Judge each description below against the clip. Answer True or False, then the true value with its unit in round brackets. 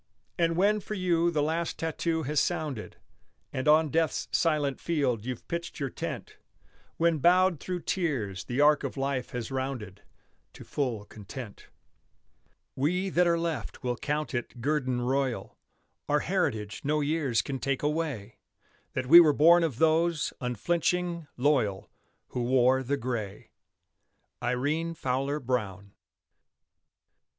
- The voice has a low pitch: False (145 Hz)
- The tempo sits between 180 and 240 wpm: False (135 wpm)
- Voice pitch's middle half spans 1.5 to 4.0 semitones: False (4.9 semitones)